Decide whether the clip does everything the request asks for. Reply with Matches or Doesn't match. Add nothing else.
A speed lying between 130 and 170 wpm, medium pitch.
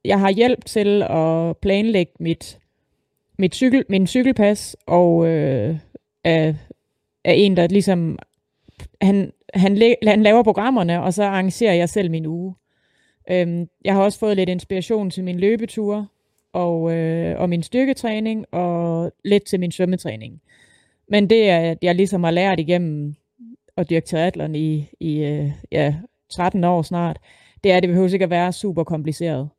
Matches